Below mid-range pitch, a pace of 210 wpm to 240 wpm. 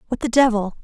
No: high, 230 Hz; fast, 215 wpm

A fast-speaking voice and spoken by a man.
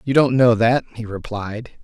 No: average, 195 wpm; male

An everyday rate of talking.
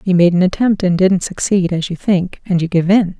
No: fast, 265 wpm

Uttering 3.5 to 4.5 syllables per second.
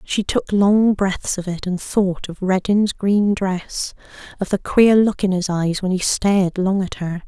Yes: 4.1 syllables/s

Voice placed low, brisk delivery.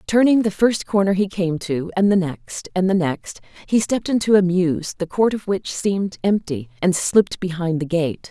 No: medium, 185 Hz; fast, 210 wpm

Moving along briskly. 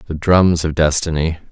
No: average, 160 wpm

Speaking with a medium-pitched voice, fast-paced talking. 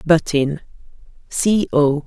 No: medium, 160 Hz; slow, 115 wpm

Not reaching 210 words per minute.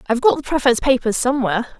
Yes: average, 200 wpm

